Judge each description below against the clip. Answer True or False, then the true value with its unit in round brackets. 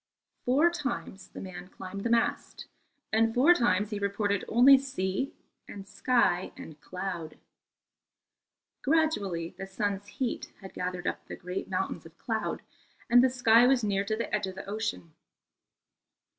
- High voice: True (205 Hz)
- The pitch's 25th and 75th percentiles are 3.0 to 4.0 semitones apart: False (4.4 semitones)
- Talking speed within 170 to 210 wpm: False (150 wpm)